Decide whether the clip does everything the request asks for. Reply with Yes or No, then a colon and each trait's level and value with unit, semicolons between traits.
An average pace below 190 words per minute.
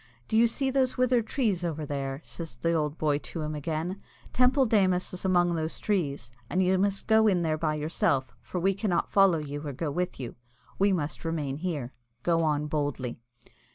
No: average, 195 wpm